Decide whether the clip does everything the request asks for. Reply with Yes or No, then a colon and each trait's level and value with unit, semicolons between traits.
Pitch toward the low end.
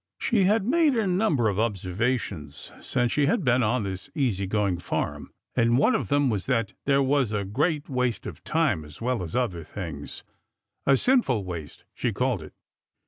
Yes: low, 120 Hz